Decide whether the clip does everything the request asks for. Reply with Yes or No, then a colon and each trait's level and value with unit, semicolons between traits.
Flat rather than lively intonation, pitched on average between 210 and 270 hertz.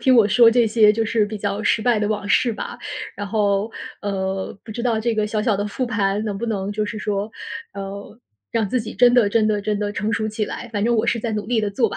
Yes: narrow, 1.9 semitones; high, 215 Hz